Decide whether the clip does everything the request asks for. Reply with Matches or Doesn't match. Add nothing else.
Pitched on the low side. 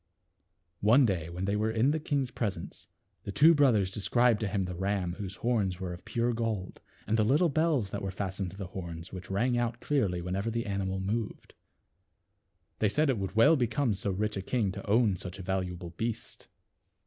Matches